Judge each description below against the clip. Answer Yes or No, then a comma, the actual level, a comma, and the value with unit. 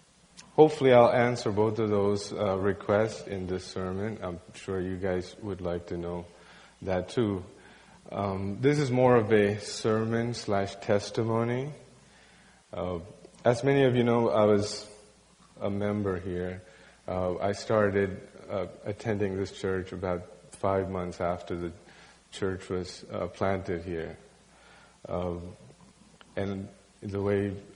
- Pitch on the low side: Yes, low, 100 Hz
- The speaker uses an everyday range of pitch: Yes, average, 3.1 semitones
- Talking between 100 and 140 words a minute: Yes, slow, 135 wpm